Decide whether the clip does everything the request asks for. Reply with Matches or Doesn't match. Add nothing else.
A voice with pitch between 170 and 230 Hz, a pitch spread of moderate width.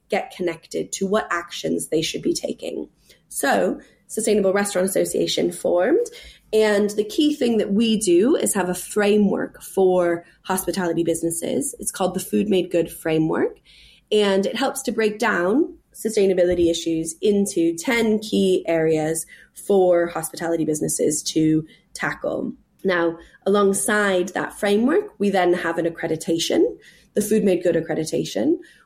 Matches